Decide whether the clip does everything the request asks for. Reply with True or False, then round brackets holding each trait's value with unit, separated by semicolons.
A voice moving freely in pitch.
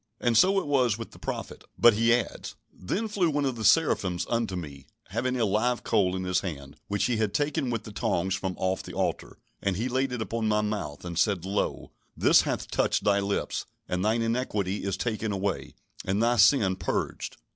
False (4.2 semitones)